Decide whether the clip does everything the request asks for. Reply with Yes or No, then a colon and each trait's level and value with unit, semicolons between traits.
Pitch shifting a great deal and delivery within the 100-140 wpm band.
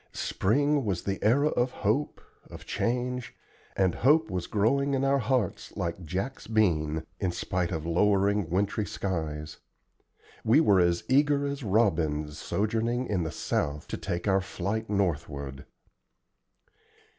Yes: wide, 6.1 semitones; slow, 135 wpm